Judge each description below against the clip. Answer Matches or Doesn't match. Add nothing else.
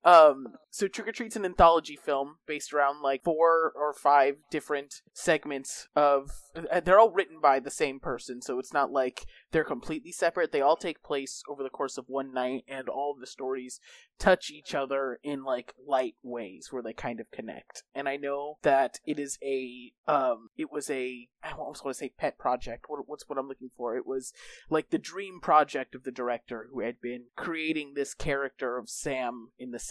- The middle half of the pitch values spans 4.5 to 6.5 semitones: Doesn't match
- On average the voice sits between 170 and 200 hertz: Doesn't match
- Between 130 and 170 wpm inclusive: Doesn't match